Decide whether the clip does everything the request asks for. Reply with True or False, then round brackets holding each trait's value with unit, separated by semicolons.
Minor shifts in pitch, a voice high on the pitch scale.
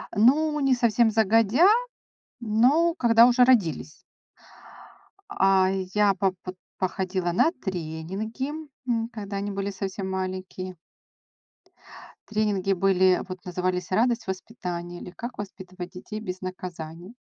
False (3.7 semitones; 195 Hz)